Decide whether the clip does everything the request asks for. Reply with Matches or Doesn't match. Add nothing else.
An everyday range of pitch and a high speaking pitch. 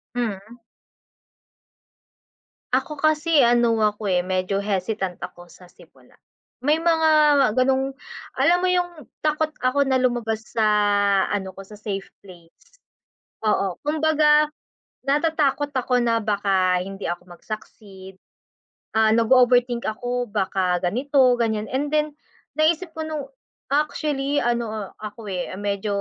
Doesn't match